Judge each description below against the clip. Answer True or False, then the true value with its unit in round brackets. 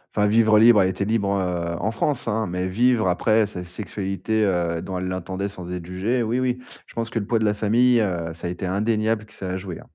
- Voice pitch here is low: True (100 Hz)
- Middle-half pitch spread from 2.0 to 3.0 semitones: False (3.4 semitones)